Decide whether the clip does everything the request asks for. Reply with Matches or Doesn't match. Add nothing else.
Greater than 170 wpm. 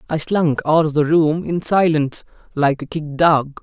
Matches